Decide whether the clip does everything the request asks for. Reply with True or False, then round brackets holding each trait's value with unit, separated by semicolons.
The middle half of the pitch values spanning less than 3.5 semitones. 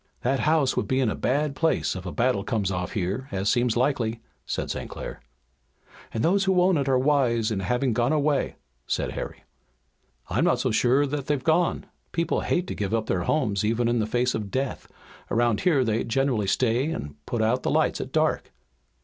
False (4.3 semitones)